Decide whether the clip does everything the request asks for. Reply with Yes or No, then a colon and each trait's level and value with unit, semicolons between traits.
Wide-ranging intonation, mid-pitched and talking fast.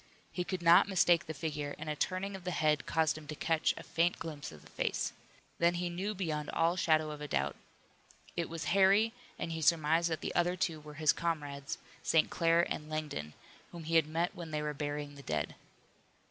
No: narrow, 2.4 semitones; medium, 160 Hz; fast, 210 wpm